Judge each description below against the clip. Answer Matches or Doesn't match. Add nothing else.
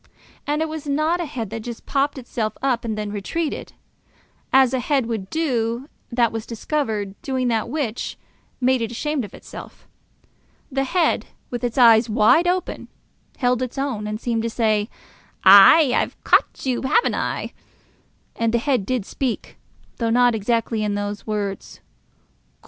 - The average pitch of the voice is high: Matches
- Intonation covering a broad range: Doesn't match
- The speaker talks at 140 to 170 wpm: Matches